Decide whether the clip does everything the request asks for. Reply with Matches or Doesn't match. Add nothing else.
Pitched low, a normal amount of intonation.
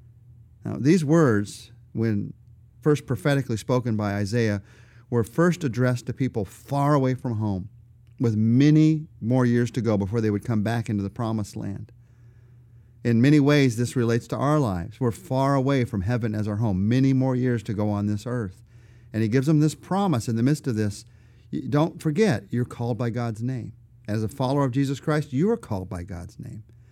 Matches